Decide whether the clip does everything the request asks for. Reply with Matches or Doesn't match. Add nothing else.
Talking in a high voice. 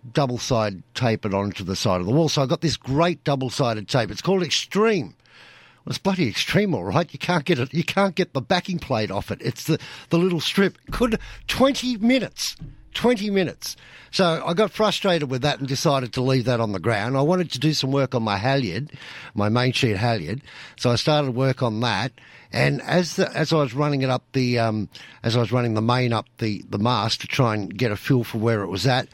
Doesn't match